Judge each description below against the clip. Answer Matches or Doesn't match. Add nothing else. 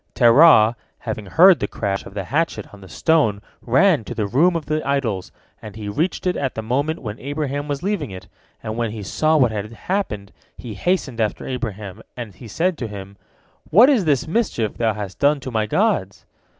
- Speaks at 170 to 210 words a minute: Matches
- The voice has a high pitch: Doesn't match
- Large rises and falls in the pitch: Matches